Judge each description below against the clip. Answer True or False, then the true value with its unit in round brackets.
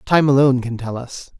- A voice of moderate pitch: False (130 Hz)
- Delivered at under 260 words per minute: True (215 wpm)